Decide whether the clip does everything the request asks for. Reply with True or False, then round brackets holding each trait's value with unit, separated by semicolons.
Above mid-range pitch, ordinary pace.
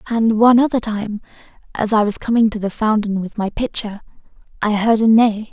True (220 Hz; 195 wpm)